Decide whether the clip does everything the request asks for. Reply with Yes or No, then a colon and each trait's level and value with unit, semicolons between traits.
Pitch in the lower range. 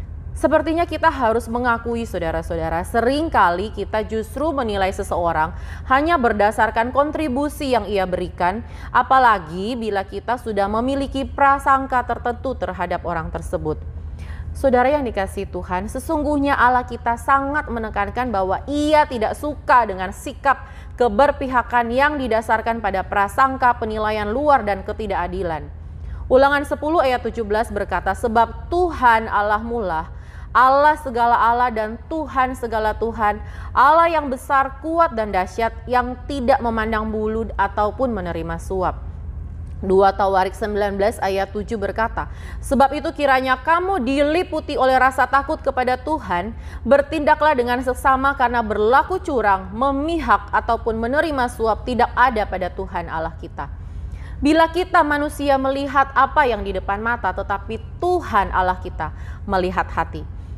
No: high, 235 Hz